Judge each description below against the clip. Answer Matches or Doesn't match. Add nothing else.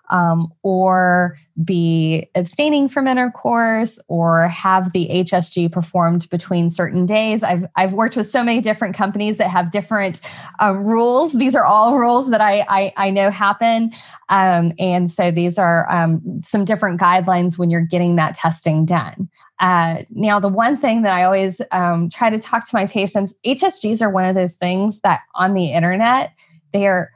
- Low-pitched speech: Doesn't match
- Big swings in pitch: Doesn't match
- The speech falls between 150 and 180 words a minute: Matches